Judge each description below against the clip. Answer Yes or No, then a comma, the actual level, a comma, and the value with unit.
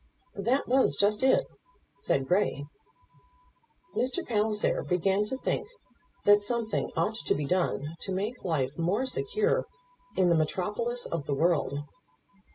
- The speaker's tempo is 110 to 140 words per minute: Yes, slow, 135 wpm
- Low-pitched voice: No, high, 205 Hz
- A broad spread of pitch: Yes, wide, 6.1 semitones